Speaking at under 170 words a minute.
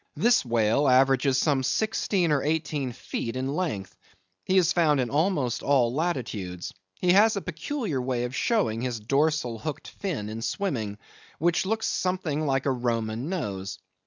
Yes: average, 160 wpm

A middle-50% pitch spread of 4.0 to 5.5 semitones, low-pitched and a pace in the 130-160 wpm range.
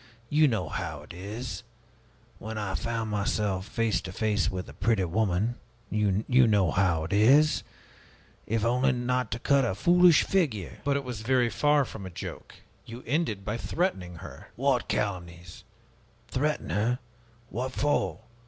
Yes: average, 4.9 semitones; low, 110 Hz; average, 155 wpm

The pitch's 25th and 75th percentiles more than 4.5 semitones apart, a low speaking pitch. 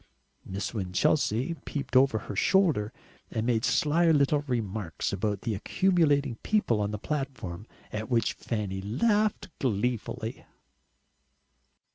Yes: wide, 5.5 semitones; low, 115 Hz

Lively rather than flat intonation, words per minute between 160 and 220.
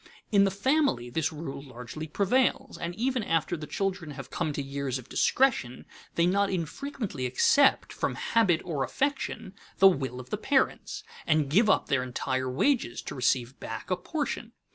Yes: wide, 7.9 semitones; average, 170 wpm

